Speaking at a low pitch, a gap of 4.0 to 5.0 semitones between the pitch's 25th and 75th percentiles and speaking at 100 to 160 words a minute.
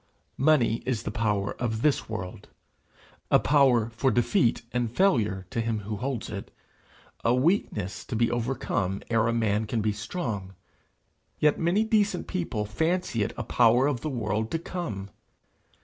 Yes: low, 115 Hz; average, 4.6 semitones; average, 155 wpm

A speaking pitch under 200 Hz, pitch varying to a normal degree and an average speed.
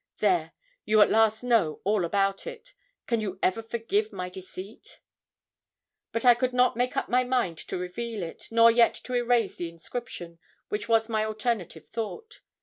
No: high, 225 Hz; average, 3.8 semitones; average, 170 wpm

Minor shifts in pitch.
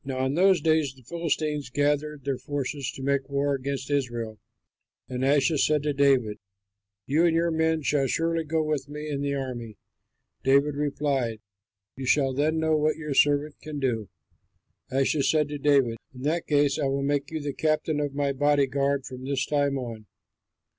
Yes: narrow, 2.1 semitones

